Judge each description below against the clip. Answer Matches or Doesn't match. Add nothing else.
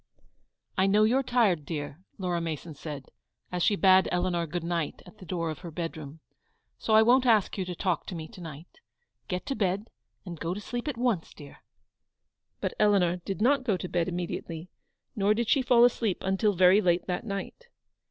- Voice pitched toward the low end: Doesn't match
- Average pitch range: Matches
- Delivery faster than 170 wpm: Matches